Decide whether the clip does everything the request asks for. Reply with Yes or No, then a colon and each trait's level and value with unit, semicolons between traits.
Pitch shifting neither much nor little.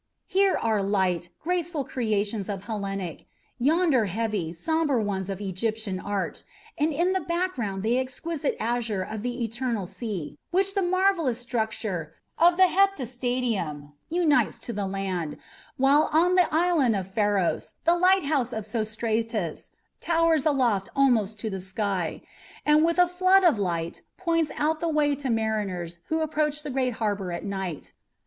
No: wide, 8.1 semitones